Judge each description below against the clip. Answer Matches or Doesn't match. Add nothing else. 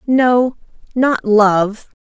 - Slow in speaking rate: Matches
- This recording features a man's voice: Doesn't match